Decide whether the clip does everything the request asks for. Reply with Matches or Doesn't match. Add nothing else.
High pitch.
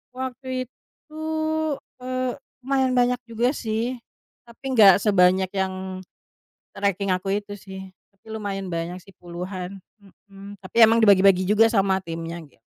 Matches